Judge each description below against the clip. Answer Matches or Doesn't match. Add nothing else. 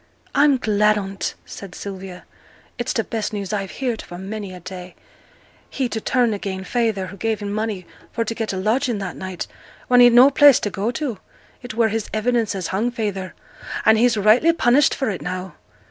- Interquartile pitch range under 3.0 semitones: Doesn't match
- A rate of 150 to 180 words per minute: Doesn't match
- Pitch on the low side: Doesn't match